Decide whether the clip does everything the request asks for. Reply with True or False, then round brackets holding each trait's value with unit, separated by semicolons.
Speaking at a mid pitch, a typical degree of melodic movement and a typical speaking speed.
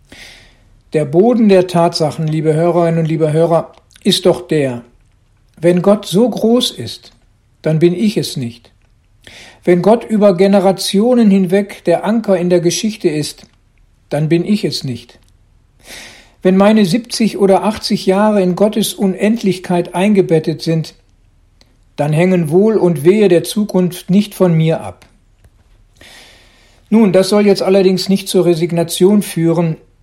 False (175 Hz; 7.7 semitones; 140 wpm)